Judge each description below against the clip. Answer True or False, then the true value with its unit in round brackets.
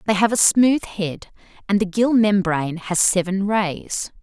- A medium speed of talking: True (170 wpm)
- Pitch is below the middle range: False (200 Hz)